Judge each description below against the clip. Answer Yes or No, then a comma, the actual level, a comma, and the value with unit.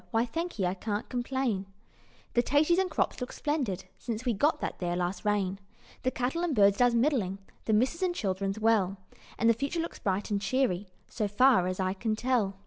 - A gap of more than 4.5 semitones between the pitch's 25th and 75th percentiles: Yes, average, 5.1 semitones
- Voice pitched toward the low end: No, high, 225 Hz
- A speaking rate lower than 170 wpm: No, average, 200 wpm